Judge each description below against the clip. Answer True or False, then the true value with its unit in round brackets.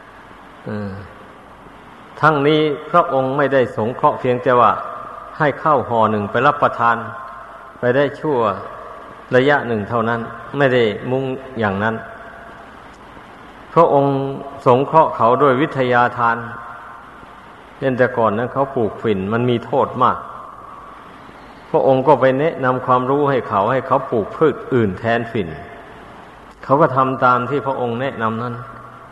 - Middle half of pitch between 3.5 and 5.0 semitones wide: False (2.7 semitones)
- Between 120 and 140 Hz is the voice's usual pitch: True (125 Hz)